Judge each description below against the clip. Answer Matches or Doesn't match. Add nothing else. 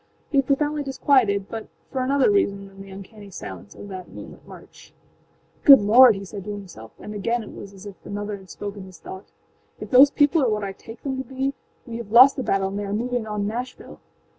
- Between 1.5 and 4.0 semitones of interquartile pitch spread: Doesn't match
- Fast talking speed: Matches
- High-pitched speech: Matches